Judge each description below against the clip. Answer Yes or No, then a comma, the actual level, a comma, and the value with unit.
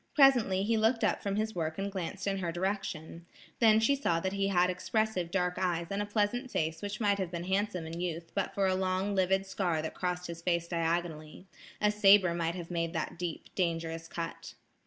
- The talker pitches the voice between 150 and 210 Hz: Yes, medium, 185 Hz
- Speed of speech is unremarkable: No, fast, 210 wpm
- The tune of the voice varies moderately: Yes, average, 3.1 semitones